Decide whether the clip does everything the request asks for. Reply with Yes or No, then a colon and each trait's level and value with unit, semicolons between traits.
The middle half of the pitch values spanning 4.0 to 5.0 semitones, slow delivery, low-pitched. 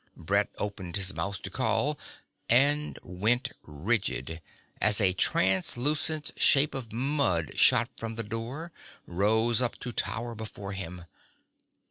Yes: average, 4.7 semitones; slow, 125 wpm; low, 110 Hz